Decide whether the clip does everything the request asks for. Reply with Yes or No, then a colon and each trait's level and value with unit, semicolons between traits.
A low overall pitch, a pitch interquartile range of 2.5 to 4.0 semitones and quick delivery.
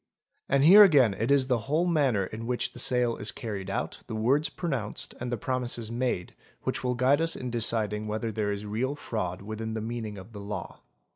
Yes: low, 115 Hz; average, 3.4 semitones; fast, 210 wpm